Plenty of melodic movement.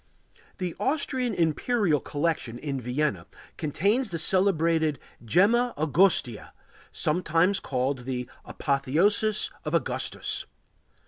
Yes: wide, 6.3 semitones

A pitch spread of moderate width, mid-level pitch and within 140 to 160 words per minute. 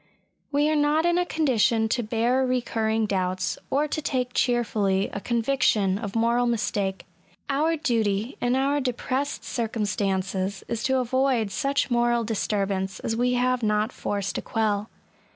No: average, 4.0 semitones; high, 235 Hz; average, 150 wpm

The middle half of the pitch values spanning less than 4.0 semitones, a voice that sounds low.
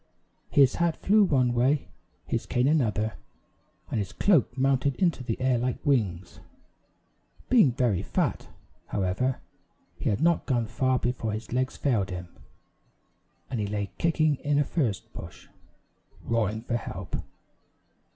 No: average, 4.6 semitones; low, 125 Hz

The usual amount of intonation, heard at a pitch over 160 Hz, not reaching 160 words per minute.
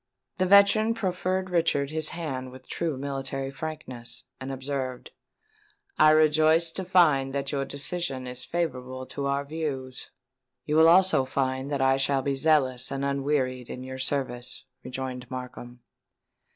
No: average, 3.4 semitones; medium, 140 Hz; average, 145 wpm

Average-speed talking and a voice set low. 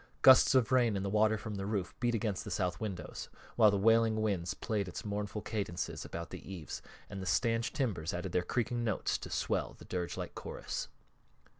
Yes: average, 195 wpm; low, 105 Hz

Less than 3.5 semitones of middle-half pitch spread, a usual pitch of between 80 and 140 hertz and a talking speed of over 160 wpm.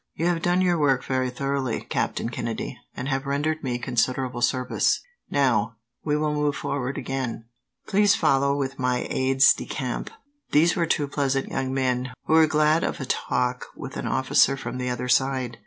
Yes: average, 2.8 semitones; low, 135 Hz; average, 180 wpm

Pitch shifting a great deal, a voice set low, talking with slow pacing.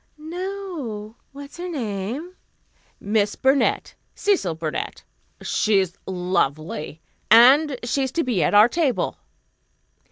No: wide, 7.6 semitones; high, 240 Hz; slow, 100 wpm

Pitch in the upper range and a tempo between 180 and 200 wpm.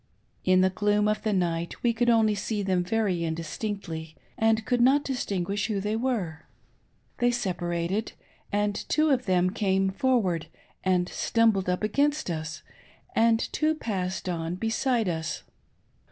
No: high, 205 Hz; average, 145 wpm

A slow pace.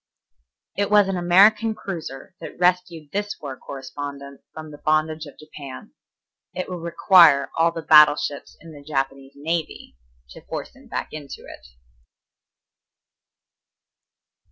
Yes: slow, 130 wpm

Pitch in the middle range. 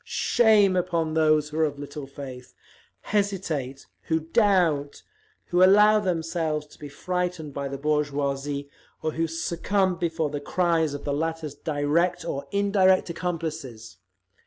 Yes: medium, 160 Hz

